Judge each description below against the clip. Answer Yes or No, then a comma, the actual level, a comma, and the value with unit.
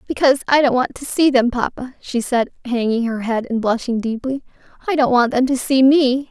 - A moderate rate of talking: No, fast, 220 wpm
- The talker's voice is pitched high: Yes, very high, 255 Hz